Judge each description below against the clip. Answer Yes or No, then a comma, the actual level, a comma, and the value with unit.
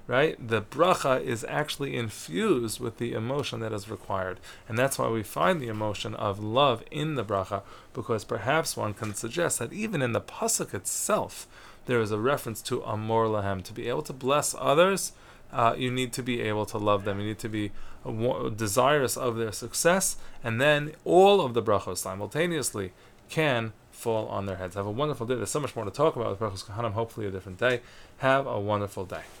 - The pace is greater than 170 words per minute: Yes, average, 200 wpm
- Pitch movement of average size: Yes, average, 4.1 semitones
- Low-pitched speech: Yes, low, 115 Hz